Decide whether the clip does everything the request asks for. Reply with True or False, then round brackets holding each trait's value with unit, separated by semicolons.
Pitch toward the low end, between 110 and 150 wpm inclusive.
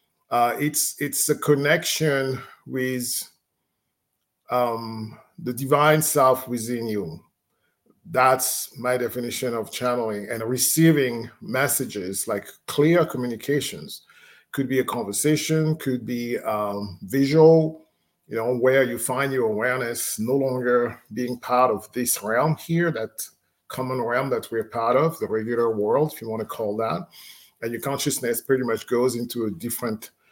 True (125 Hz; 140 wpm)